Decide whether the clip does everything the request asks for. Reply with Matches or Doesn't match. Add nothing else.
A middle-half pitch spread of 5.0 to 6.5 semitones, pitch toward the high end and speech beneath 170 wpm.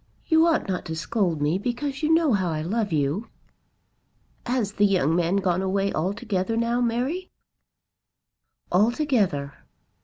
Matches